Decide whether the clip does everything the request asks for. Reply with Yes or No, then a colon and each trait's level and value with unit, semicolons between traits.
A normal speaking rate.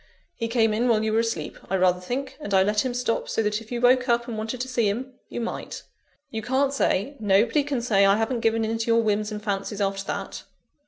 No: fast, 250 wpm